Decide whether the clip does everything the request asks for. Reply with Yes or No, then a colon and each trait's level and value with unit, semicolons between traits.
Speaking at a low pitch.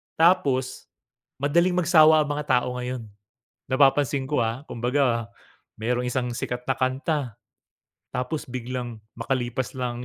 Yes: low, 130 Hz